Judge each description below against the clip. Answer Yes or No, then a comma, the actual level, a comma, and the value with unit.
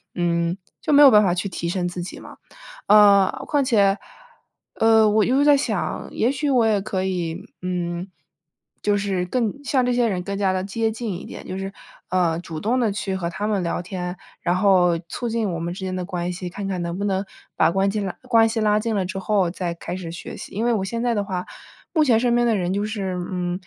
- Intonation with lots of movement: No, average, 3.7 semitones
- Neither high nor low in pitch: No, high, 195 Hz